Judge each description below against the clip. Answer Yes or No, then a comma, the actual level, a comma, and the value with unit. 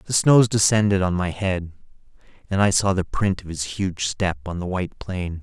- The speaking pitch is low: Yes, very low, 95 Hz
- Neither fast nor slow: No, fast, 210 wpm